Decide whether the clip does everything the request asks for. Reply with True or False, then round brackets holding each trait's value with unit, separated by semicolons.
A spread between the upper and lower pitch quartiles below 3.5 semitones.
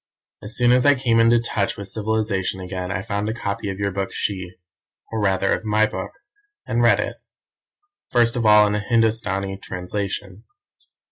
True (2.6 semitones)